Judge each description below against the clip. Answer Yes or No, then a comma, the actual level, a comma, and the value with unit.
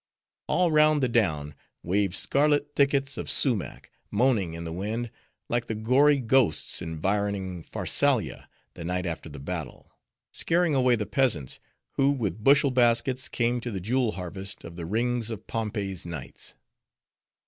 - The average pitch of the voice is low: Yes, low, 110 Hz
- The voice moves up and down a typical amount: No, wide, 6.4 semitones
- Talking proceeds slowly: No, average, 150 wpm